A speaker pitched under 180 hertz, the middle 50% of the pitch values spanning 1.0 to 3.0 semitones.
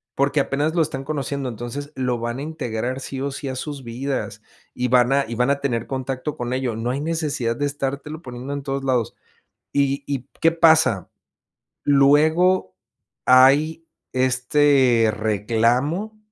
Yes: low, 135 Hz; average, 2.7 semitones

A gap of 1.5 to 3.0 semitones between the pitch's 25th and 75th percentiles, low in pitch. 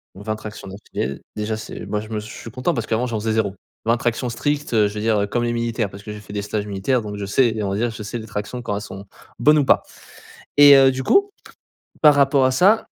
No: average, 3.5 semitones; low, 110 Hz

